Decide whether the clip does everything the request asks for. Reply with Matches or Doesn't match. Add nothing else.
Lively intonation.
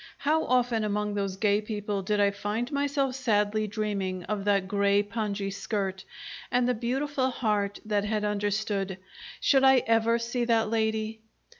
Doesn't match